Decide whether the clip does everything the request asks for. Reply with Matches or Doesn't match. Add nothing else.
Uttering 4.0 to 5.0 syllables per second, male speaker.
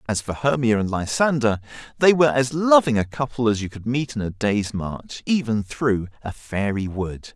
Matches